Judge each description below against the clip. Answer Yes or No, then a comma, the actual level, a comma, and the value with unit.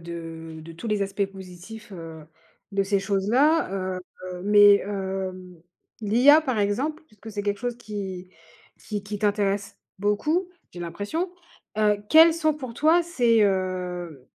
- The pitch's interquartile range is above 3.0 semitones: Yes, average, 3.8 semitones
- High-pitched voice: Yes, high, 205 Hz